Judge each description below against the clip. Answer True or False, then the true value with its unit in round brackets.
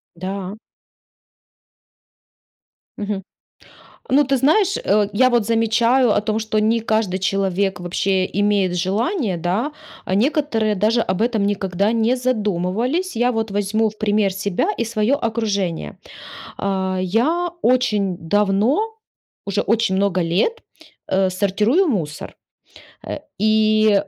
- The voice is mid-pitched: False (210 Hz)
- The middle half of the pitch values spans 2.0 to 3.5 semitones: True (3.2 semitones)